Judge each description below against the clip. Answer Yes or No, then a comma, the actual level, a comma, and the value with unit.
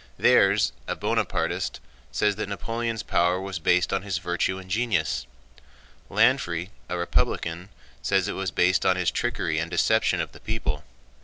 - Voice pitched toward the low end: Yes, very low, 90 Hz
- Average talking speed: Yes, average, 155 wpm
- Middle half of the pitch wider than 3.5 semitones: No, average, 2.8 semitones